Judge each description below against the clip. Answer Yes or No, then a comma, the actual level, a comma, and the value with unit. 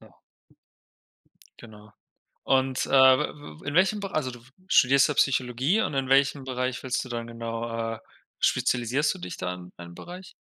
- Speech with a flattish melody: No, average, 3.1 semitones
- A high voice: No, low, 130 Hz